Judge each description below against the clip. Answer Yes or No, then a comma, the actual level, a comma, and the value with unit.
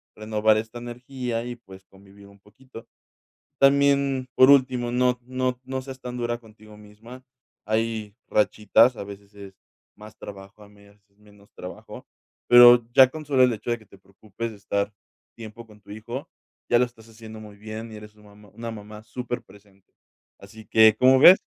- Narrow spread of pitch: No, average, 3.0 semitones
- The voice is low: Yes, low, 110 Hz